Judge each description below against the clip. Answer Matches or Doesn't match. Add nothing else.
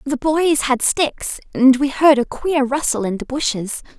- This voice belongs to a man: Doesn't match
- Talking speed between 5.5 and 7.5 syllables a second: Doesn't match